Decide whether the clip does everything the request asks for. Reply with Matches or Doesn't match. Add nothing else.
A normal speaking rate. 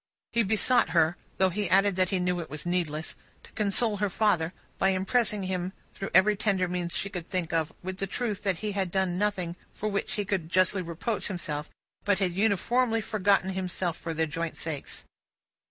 Matches